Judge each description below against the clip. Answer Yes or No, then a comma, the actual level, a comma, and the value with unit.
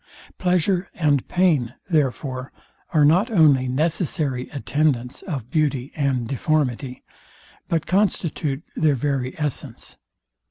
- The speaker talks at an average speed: No, slow, 105 wpm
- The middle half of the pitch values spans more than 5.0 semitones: No, average, 3.8 semitones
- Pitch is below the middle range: No, medium, 145 Hz